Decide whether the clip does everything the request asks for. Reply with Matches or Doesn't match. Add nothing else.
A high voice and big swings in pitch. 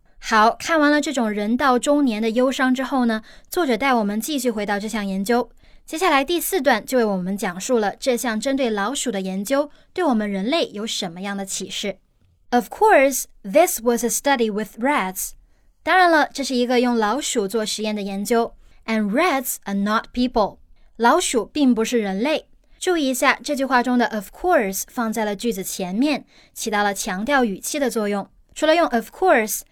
Doesn't match